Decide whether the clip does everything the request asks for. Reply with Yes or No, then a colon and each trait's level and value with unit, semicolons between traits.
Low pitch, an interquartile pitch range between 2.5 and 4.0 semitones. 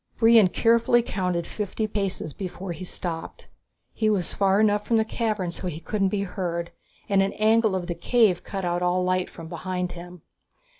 No: high, 190 Hz; average, 3.2 semitones